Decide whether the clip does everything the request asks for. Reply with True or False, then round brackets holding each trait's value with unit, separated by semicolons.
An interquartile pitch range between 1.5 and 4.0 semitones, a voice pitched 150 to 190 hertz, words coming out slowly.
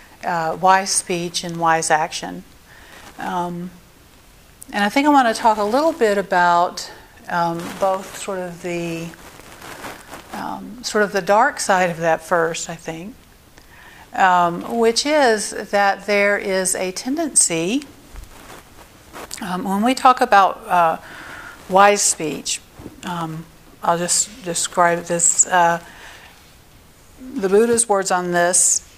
True (3.6 semitones; 185 Hz; 125 wpm)